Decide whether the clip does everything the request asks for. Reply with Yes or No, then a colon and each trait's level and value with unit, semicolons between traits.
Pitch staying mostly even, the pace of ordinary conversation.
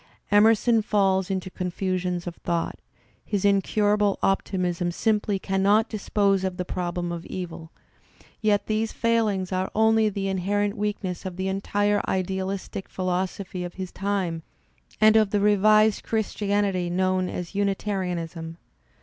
No: narrow, 2.2 semitones; slow, 130 wpm